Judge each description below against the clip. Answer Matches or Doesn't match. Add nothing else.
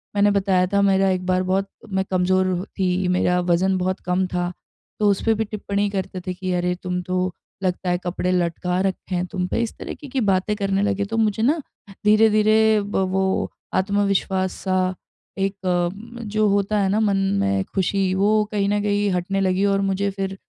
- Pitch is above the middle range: Matches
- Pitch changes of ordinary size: Doesn't match